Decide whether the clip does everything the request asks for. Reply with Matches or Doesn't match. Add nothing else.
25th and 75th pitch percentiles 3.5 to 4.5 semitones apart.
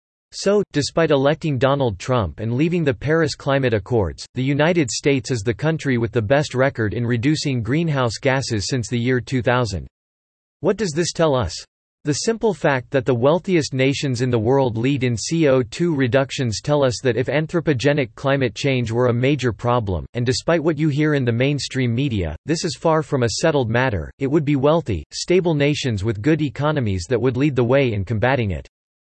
Matches